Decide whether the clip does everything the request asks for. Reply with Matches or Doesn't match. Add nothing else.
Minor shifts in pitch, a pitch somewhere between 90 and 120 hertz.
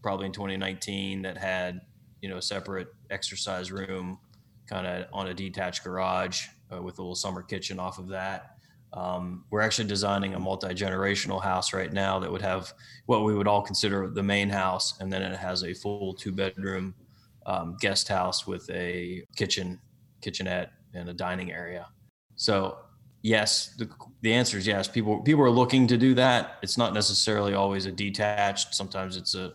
Matches